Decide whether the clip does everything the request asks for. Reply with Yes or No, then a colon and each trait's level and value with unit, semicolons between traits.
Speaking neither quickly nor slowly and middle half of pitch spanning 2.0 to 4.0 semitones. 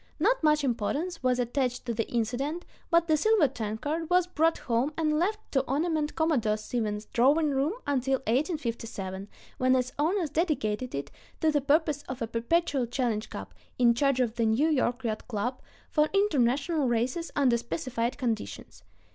No: average, 165 wpm; average, 4.9 semitones